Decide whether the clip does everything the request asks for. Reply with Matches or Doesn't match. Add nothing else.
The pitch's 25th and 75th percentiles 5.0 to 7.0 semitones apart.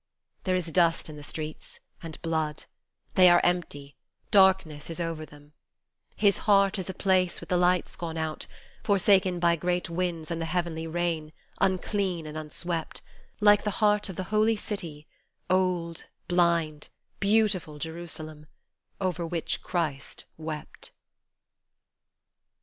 Doesn't match